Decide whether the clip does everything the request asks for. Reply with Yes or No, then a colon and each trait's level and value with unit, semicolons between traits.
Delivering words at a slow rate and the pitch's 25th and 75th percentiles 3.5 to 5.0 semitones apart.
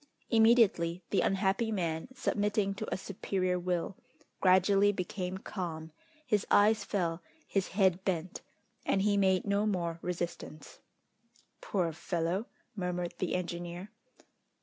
No: slow, 120 wpm; narrow, 2.6 semitones